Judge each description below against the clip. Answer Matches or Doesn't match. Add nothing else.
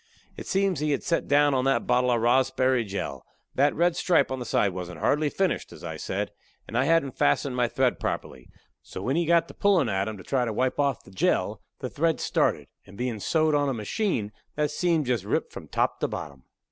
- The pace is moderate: Doesn't match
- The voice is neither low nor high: Doesn't match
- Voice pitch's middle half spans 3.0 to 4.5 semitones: Doesn't match